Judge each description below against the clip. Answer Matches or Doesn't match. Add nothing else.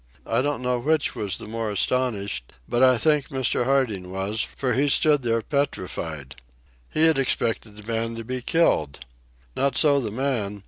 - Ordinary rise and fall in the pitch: Matches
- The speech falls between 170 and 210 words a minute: Matches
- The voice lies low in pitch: Matches